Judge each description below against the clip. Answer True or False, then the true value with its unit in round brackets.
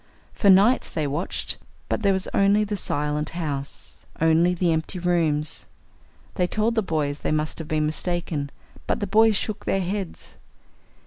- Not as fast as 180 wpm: True (165 wpm)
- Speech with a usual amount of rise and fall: True (4.4 semitones)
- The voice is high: False (175 Hz)